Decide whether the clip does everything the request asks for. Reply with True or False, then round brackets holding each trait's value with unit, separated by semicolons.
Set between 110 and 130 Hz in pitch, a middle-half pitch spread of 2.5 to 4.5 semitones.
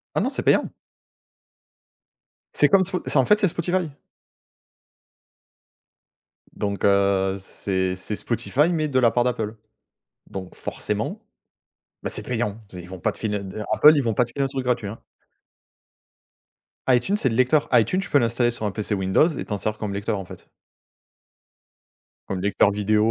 False (115 Hz; 5.0 semitones)